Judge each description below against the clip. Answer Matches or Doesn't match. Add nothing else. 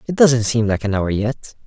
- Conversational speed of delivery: Doesn't match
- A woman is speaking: Doesn't match